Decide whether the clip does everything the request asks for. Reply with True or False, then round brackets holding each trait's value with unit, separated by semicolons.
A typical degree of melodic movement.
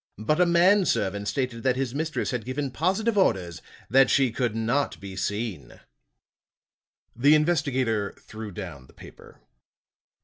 False (6.2 semitones)